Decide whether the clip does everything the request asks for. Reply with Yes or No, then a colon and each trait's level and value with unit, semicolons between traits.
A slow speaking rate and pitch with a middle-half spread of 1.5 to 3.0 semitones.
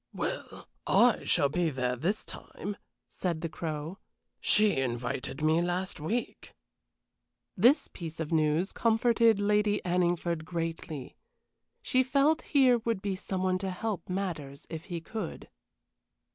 No: slow, 130 wpm; average, 4.8 semitones